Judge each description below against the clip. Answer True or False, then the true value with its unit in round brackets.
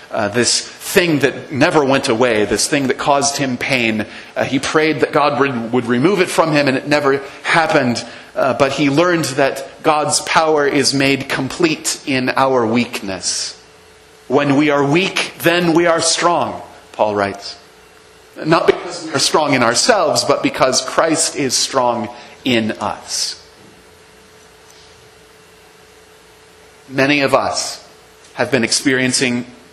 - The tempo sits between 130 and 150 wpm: True (145 wpm)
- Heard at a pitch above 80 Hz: True (140 Hz)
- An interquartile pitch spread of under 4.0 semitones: True (3.4 semitones)